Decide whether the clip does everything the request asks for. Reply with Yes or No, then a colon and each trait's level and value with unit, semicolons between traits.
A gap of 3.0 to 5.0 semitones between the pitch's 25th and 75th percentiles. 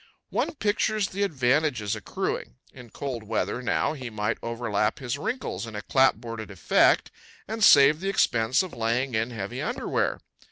No: wide, 5.4 semitones